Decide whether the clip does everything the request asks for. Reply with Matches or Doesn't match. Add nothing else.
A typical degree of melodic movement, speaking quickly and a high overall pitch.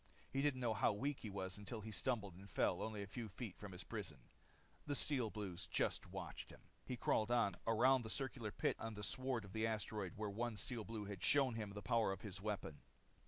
Doesn't match